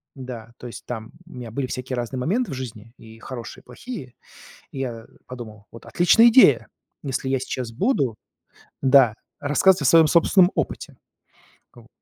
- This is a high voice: No, low, 130 Hz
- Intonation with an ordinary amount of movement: Yes, average, 4.8 semitones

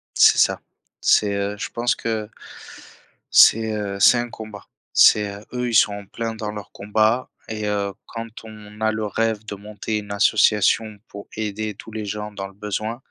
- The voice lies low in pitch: Yes, low, 105 Hz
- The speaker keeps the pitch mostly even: Yes, narrow, 1.4 semitones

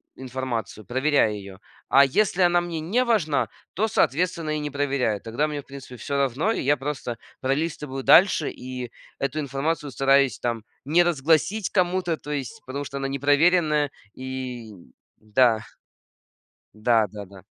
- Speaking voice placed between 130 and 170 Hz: Yes, medium, 140 Hz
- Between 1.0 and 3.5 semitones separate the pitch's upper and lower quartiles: No, average, 4.1 semitones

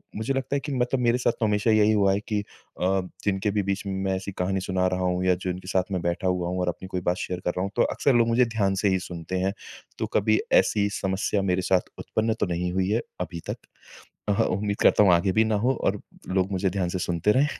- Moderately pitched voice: No, very low, 95 Hz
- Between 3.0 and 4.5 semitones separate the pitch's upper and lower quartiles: No, narrow, 2.5 semitones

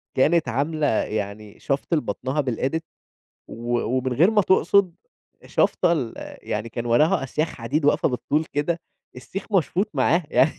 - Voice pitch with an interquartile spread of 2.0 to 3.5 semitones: No, wide, 5.5 semitones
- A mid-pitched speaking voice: Yes, medium, 145 Hz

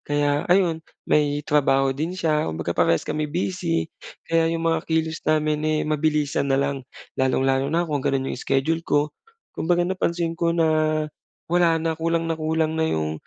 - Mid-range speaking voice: Yes, medium, 155 Hz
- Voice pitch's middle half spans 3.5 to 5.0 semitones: No, narrow, 2.4 semitones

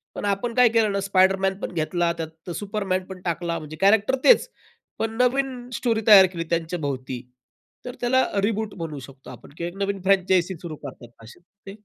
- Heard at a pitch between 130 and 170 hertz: No, high, 190 Hz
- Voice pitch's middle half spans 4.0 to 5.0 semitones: Yes, average, 4.5 semitones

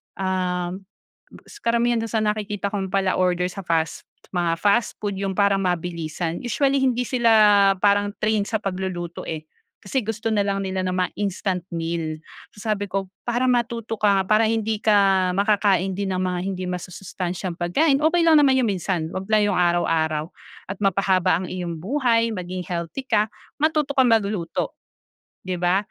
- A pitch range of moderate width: Yes, average, 3.6 semitones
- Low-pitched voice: No, high, 195 Hz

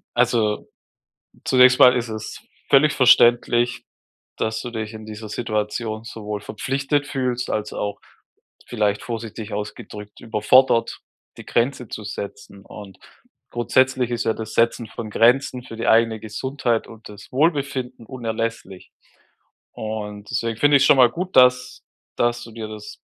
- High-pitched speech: No, low, 115 Hz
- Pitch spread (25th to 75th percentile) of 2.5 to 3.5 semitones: Yes, average, 2.8 semitones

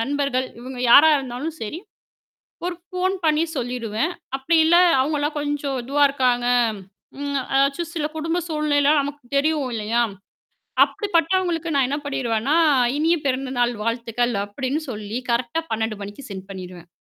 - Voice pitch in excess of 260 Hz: Yes, very high, 275 Hz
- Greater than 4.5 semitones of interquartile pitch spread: No, average, 4.2 semitones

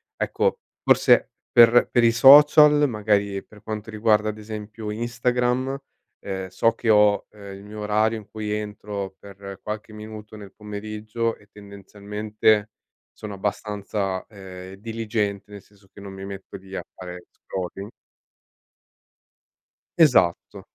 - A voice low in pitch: Yes, low, 105 Hz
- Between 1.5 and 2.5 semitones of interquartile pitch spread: Yes, narrow, 1.8 semitones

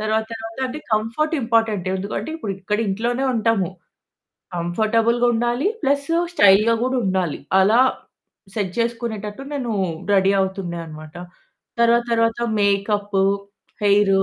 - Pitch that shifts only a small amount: No, average, 3.2 semitones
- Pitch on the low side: No, high, 215 Hz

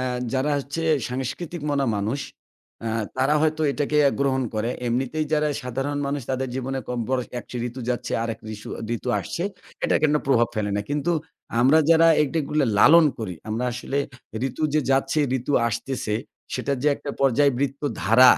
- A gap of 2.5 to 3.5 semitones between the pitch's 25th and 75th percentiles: Yes, average, 2.9 semitones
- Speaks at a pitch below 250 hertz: Yes, low, 135 Hz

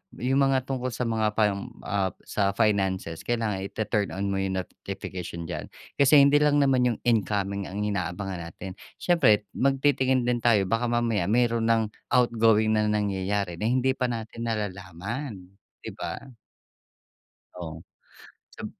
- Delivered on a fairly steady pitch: No, average, 3.9 semitones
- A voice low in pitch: Yes, low, 110 Hz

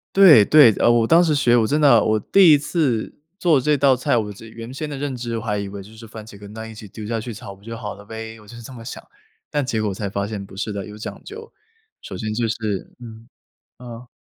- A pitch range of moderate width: Yes, average, 3.7 semitones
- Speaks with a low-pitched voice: Yes, low, 115 Hz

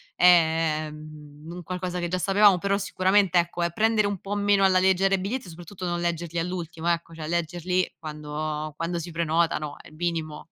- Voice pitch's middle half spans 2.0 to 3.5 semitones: Yes, narrow, 2.6 semitones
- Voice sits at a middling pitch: Yes, medium, 175 Hz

